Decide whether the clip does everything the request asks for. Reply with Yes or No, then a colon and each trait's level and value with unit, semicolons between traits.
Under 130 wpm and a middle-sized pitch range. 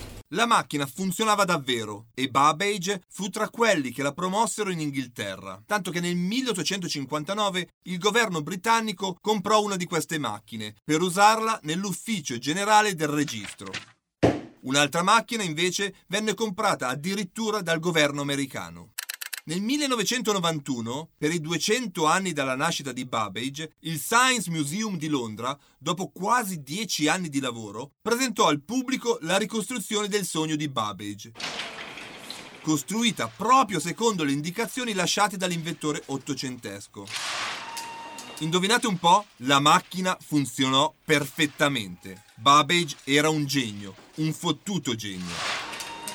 No: average, 120 wpm; wide, 6.7 semitones